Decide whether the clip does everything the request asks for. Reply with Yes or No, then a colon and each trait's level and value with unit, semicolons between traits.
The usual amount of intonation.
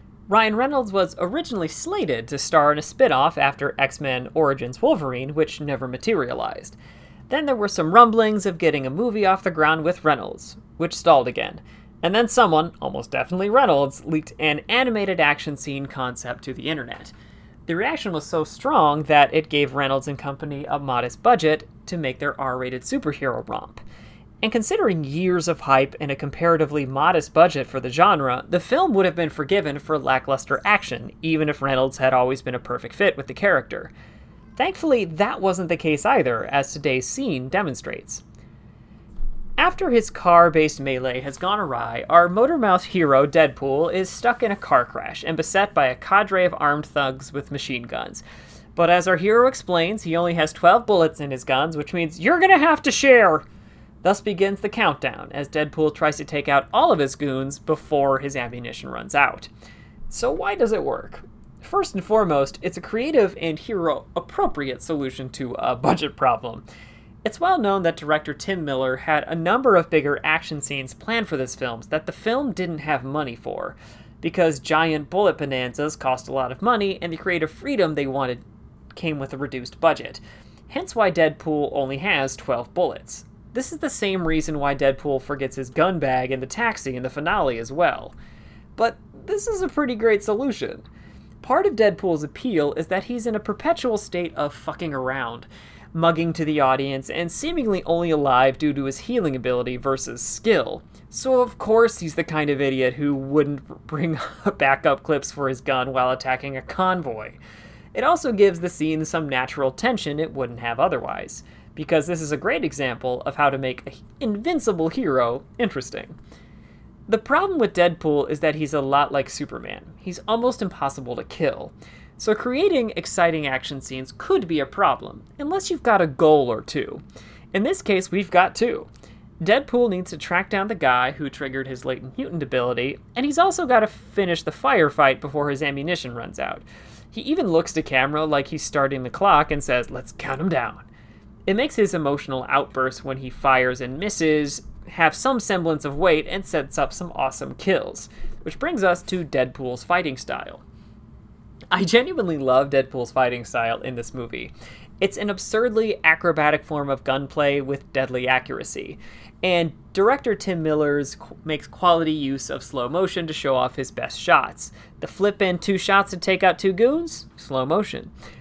No: wide, 6.1 semitones